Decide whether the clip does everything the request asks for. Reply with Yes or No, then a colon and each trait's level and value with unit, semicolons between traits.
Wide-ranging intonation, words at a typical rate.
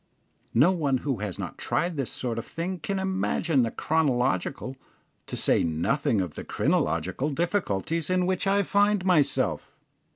Yes: wide, 7.0 semitones; average, 155 wpm